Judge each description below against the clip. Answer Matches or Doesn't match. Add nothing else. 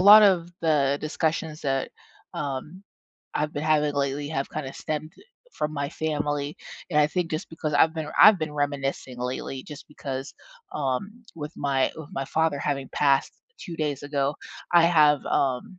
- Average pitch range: Doesn't match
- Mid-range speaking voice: Matches